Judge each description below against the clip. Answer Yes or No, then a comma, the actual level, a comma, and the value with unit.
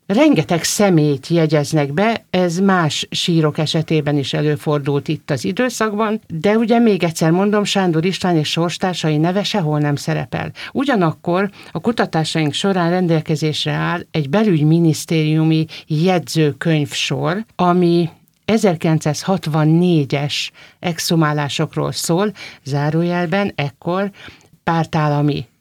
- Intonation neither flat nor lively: Yes, average, 3.4 semitones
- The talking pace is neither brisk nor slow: No, slow, 100 wpm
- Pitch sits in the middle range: Yes, medium, 165 Hz